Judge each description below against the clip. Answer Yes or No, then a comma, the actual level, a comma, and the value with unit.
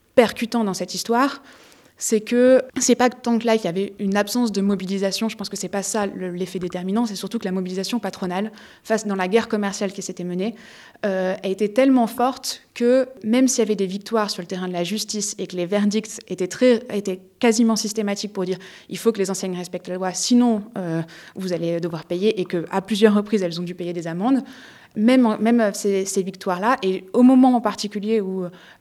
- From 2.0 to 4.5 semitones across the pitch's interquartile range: Yes, average, 3.6 semitones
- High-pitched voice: Yes, high, 205 Hz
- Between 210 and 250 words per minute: Yes, average, 215 wpm